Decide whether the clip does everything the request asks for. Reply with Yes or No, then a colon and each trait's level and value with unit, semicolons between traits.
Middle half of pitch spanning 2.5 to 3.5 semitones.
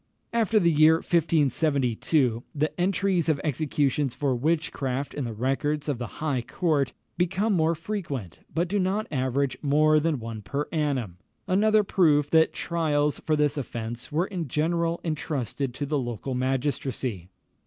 No: average, 4.0 semitones